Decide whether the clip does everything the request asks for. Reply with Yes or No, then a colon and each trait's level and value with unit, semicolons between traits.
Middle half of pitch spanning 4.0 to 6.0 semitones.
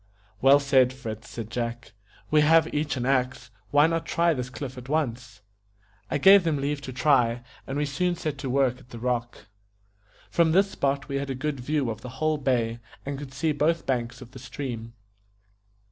No: average, 3.2 semitones